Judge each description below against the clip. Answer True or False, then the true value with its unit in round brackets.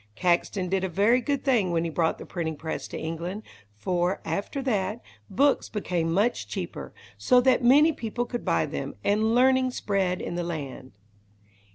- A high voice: True (195 Hz)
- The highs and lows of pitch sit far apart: True (6.0 semitones)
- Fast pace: False (175 wpm)